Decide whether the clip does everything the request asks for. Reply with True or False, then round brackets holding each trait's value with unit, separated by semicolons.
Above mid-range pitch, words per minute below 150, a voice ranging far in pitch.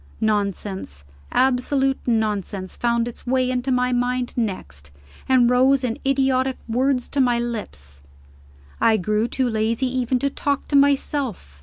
False (245 Hz; 140 wpm; 3.2 semitones)